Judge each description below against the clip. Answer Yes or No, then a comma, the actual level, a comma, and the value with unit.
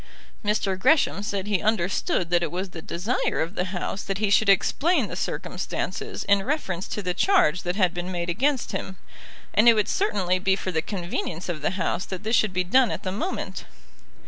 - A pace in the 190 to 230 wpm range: Yes, fast, 205 wpm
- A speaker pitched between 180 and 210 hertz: Yes, high, 190 Hz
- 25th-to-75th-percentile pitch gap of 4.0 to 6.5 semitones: No, average, 3.2 semitones